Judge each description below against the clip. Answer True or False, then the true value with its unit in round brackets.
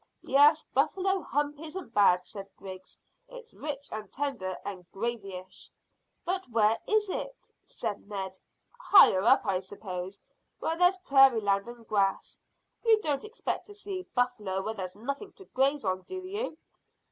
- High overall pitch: True (245 Hz)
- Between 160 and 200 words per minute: False (150 wpm)